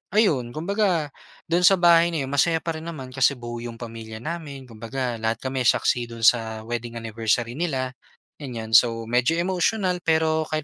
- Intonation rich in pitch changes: Yes, wide, 6.0 semitones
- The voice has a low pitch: Yes, low, 130 Hz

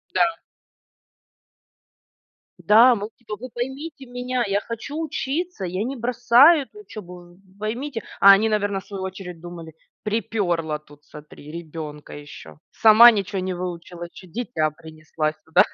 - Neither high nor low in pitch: No, high, 205 Hz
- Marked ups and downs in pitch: Yes, wide, 6.1 semitones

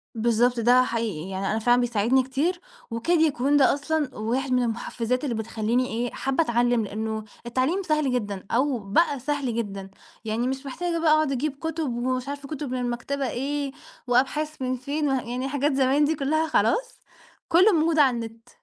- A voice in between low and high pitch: No, very high, 255 Hz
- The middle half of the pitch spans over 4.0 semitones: No, average, 3.7 semitones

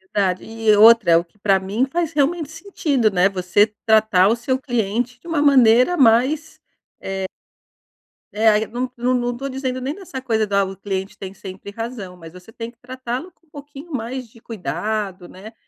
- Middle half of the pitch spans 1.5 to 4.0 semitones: No, average, 4.7 semitones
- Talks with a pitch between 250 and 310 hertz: No, high, 230 Hz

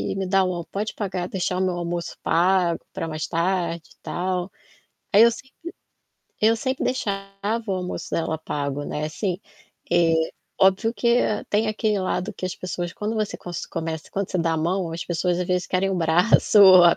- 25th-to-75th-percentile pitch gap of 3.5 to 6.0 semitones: No, average, 2.7 semitones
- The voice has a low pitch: No, medium, 185 Hz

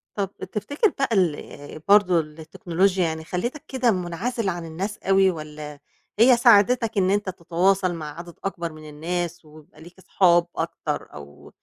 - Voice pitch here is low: No, medium, 180 Hz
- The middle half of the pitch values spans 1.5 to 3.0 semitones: No, average, 4.0 semitones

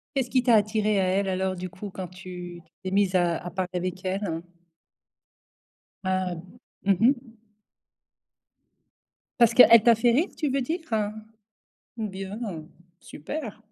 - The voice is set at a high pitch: Yes, high, 195 Hz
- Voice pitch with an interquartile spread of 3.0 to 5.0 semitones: Yes, average, 4.0 semitones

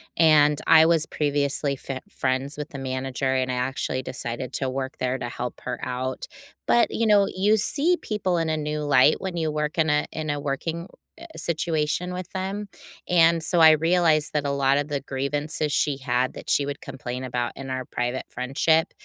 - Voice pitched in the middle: Yes, medium, 145 Hz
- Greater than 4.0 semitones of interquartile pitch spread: No, average, 3.7 semitones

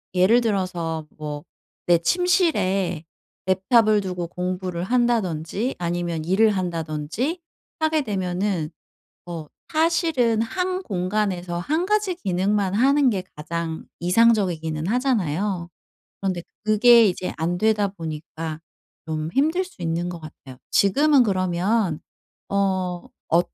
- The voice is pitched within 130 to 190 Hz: Yes, medium, 185 Hz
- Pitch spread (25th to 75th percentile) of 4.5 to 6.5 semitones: Yes, average, 5.2 semitones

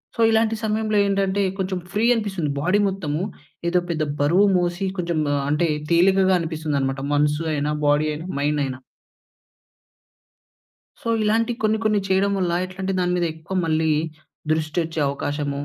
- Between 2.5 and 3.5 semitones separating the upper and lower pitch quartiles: No, average, 4.5 semitones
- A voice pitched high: No, medium, 175 Hz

